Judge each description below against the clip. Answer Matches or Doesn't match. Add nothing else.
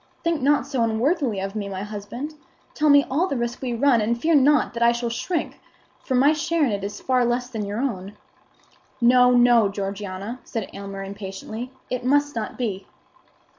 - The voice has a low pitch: Doesn't match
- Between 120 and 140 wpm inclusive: Doesn't match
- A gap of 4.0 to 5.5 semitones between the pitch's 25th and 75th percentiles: Matches